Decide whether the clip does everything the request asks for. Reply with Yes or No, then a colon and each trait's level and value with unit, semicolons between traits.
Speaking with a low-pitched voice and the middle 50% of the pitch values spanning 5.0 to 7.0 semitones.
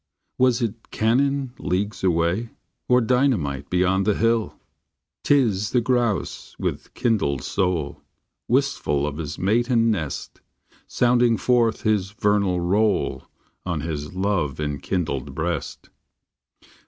Yes: low, 105 Hz; wide, 5.5 semitones